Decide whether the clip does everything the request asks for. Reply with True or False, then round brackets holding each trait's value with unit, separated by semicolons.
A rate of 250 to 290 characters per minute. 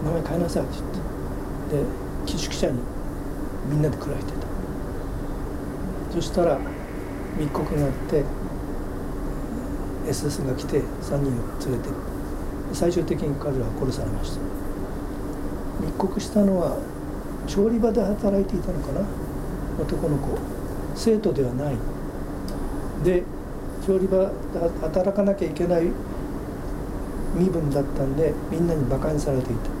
False (240 characters per minute)